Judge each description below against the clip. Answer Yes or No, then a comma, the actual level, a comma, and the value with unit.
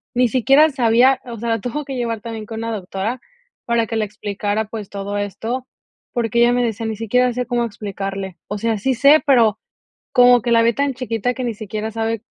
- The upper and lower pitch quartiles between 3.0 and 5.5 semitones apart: No, narrow, 2.6 semitones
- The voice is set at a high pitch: Yes, high, 230 Hz